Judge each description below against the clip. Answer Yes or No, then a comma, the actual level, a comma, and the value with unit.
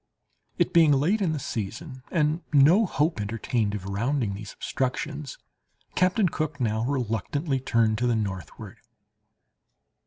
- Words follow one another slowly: Yes, slow, 130 wpm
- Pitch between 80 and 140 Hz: Yes, low, 135 Hz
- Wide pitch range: Yes, wide, 5.9 semitones